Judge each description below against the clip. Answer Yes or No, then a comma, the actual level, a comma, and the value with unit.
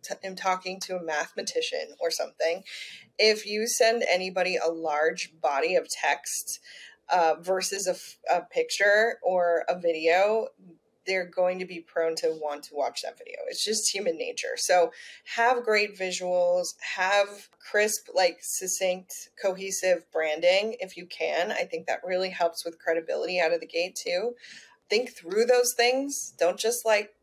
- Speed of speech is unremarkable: Yes, average, 160 wpm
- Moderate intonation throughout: No, wide, 6.9 semitones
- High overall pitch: Yes, high, 195 Hz